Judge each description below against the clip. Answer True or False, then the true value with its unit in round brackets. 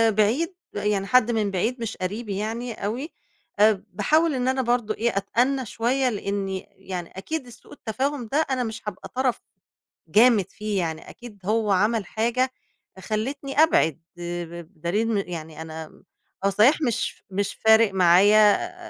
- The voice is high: True (215 Hz)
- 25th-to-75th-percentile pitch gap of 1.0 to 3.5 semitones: False (4.2 semitones)